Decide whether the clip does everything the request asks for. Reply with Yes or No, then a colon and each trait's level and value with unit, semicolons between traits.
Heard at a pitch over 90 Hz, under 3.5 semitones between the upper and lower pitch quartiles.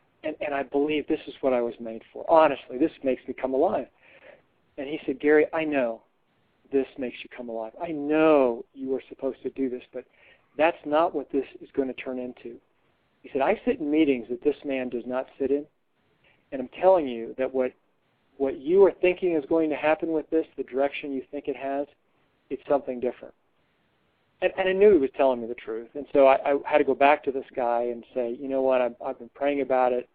Yes: low, 135 Hz; average, 2.8 semitones